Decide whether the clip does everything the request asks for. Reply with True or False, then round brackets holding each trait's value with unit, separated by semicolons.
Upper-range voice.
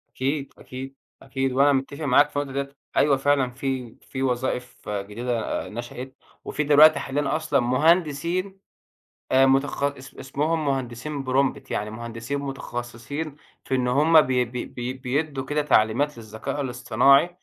False (135 Hz)